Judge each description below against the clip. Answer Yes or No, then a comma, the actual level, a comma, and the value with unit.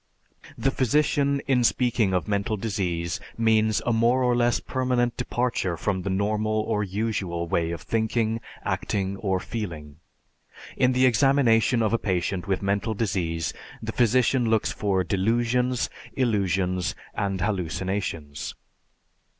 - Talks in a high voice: No, low, 110 Hz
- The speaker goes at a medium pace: No, slow, 130 wpm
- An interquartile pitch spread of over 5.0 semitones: No, average, 4.2 semitones